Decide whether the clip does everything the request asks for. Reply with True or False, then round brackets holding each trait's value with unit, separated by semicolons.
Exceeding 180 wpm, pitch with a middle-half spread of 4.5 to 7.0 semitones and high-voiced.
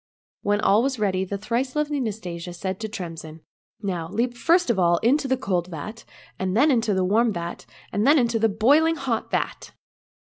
True (200 wpm; 5.4 semitones; 215 Hz)